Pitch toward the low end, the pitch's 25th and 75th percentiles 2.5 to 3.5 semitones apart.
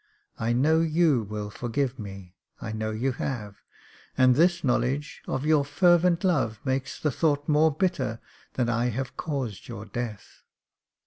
No: low, 130 Hz; wide, 5.5 semitones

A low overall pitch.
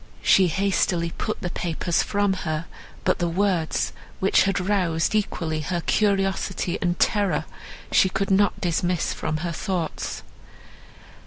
No: medium, 180 Hz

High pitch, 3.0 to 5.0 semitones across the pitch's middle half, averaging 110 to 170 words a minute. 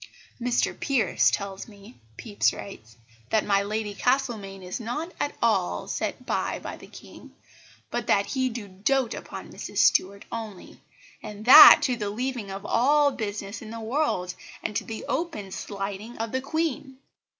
Yes: high, 220 Hz; average, 4.4 semitones; average, 160 wpm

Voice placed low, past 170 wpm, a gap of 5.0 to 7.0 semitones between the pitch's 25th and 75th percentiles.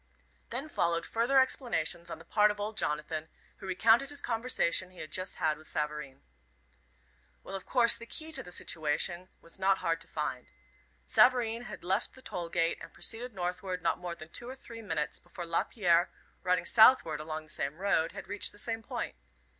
No: medium, 185 Hz; average, 190 wpm; wide, 5.6 semitones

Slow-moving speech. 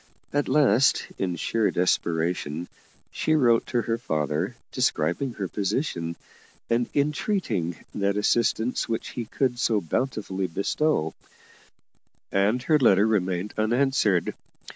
Yes: slow, 115 wpm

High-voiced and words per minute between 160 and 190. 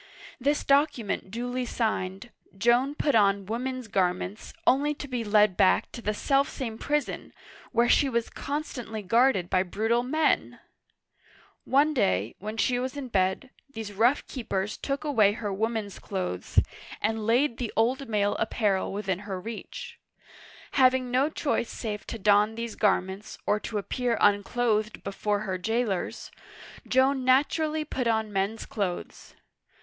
No: high, 225 Hz; average, 145 wpm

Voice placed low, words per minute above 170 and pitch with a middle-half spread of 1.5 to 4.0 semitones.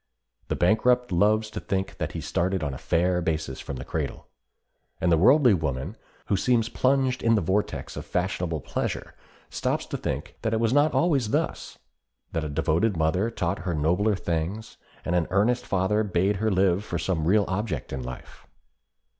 No: very low, 95 Hz; average, 180 wpm; average, 4.8 semitones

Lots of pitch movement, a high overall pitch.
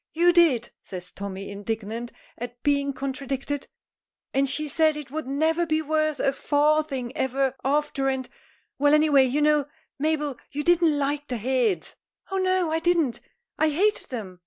No: average, 3.2 semitones; very high, 285 Hz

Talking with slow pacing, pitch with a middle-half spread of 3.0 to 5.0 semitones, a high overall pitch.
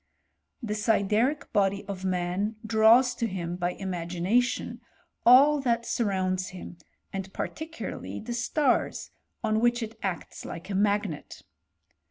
Yes: slow, 130 wpm; average, 4.3 semitones; high, 210 Hz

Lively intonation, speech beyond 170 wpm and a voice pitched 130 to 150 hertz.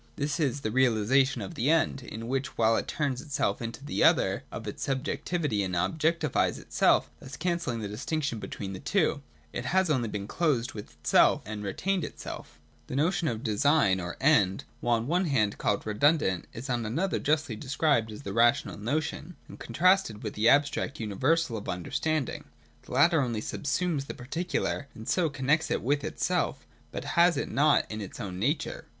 Yes: wide, 6.1 semitones; average, 185 wpm; low, 135 Hz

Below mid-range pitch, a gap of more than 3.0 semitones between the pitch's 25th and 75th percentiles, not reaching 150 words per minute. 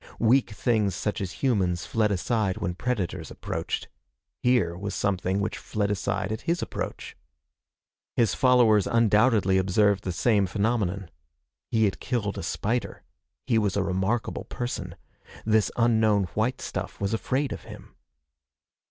Yes: low, 105 Hz; average, 3.4 semitones; average, 140 wpm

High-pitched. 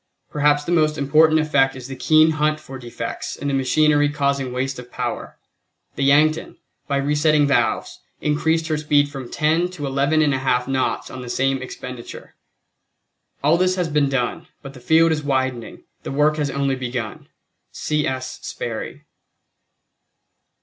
No: medium, 145 Hz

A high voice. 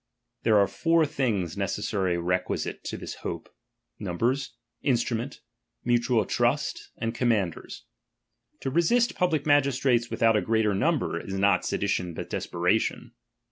No: low, 115 Hz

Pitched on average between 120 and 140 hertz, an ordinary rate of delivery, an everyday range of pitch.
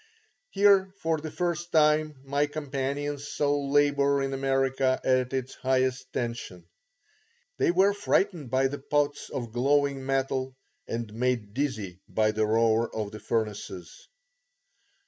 No: low, 135 Hz; slow, 130 wpm; average, 3.5 semitones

